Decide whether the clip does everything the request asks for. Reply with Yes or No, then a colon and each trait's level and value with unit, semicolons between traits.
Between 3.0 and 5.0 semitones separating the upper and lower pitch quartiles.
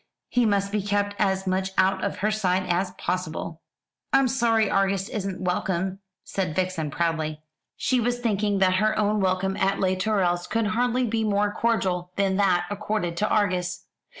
No: narrow, 2.5 semitones